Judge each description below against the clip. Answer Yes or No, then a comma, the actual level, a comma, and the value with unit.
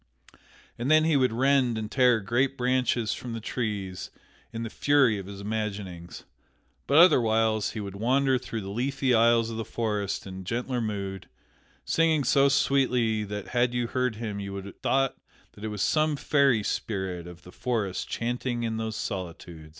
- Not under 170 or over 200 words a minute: Yes, average, 175 wpm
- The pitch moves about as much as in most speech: Yes, average, 4.1 semitones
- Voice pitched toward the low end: Yes, low, 115 Hz